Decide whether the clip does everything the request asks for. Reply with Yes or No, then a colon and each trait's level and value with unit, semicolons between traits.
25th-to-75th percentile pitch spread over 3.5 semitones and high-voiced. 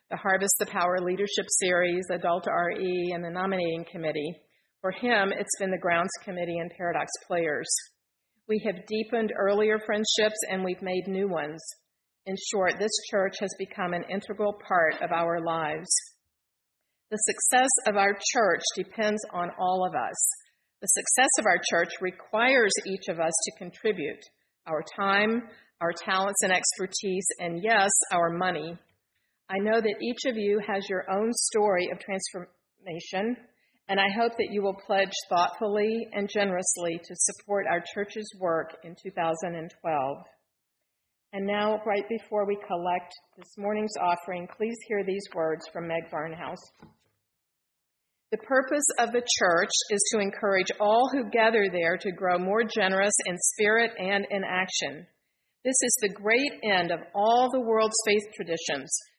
No: average, 3.2 semitones; high, 195 Hz